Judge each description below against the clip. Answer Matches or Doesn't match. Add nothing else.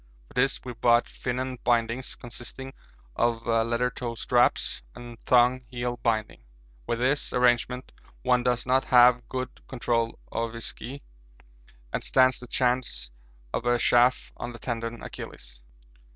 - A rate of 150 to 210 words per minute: Doesn't match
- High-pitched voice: Doesn't match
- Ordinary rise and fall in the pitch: Doesn't match